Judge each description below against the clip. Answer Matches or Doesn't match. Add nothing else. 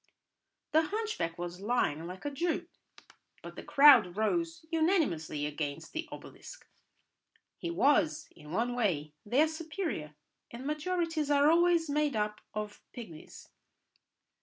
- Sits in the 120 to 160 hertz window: Doesn't match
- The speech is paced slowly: Matches